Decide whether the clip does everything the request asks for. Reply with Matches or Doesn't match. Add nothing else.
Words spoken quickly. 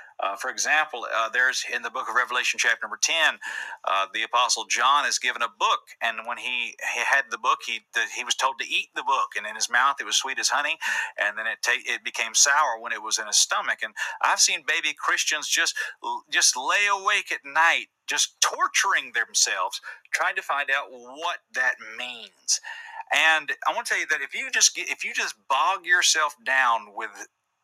Matches